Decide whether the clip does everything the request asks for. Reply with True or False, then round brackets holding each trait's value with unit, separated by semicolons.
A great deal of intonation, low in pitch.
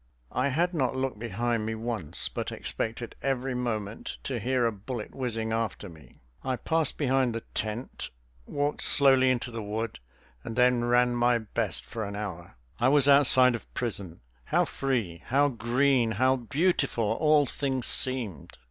False (2.9 semitones; 120 Hz)